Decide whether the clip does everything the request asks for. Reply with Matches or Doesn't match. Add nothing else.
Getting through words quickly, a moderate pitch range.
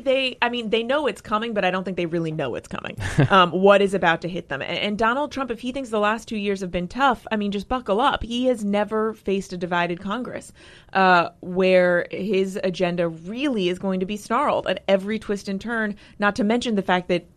Matches